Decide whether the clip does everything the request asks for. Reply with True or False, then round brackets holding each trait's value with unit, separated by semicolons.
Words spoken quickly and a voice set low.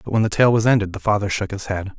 True (335 wpm; 105 Hz)